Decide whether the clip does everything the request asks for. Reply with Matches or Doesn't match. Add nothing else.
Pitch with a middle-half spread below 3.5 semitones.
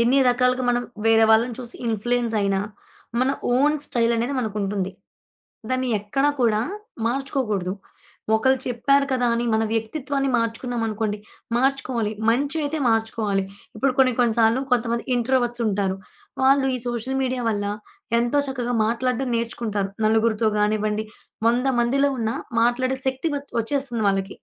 Matches